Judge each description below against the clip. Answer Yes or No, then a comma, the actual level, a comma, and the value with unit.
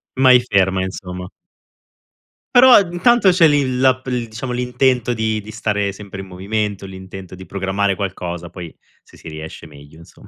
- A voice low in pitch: Yes, low, 100 Hz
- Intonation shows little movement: No, average, 5.1 semitones